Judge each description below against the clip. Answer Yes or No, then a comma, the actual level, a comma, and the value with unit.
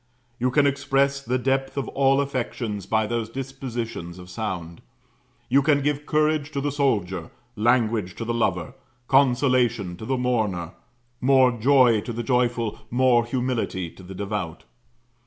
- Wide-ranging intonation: No, average, 4.1 semitones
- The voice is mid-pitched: No, low, 120 Hz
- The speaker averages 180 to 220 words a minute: No, average, 150 wpm